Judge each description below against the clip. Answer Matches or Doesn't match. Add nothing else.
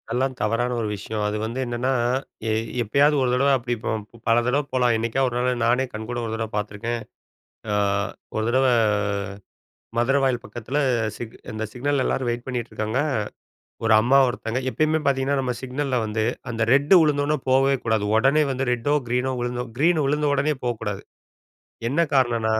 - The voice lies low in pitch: Matches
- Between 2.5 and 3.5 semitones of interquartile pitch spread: Matches